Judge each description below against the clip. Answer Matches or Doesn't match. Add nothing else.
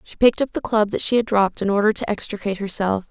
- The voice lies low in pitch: Doesn't match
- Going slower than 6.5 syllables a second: Doesn't match